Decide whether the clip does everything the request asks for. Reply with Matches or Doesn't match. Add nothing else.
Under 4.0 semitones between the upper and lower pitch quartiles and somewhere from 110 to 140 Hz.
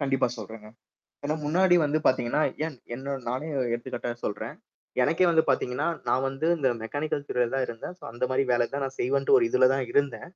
Matches